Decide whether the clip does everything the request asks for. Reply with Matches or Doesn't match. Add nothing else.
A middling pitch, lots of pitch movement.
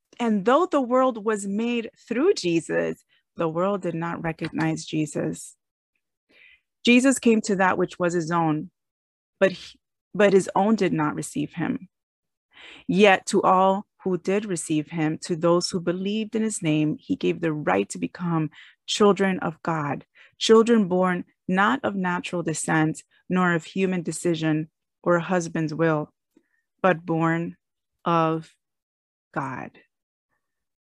Doesn't match